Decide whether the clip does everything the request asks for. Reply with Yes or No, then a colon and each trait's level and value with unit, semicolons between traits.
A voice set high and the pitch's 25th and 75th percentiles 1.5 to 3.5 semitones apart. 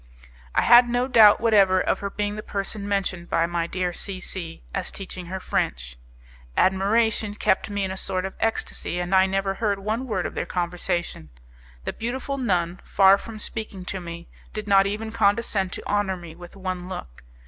Yes: high, 195 Hz; average, 2.8 semitones